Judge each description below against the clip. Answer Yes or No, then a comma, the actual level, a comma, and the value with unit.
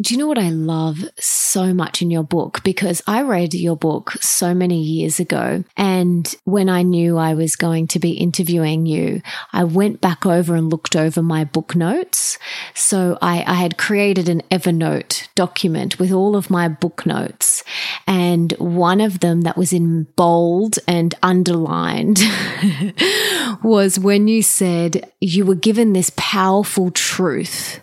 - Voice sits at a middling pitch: Yes, medium, 180 Hz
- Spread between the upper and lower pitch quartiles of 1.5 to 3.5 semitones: Yes, narrow, 2.5 semitones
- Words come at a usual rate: Yes, average, 160 wpm